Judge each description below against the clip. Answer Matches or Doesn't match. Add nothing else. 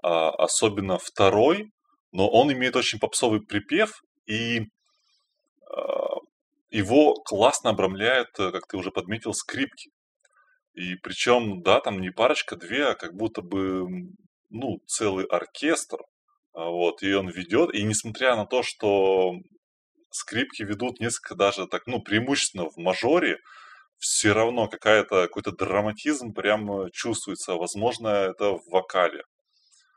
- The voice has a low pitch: Matches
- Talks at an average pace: Matches